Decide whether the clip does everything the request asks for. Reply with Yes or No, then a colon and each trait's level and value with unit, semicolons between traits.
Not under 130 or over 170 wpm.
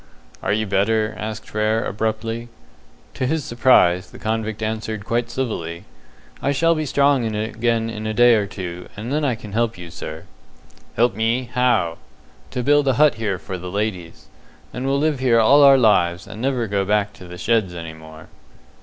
No: average, 185 wpm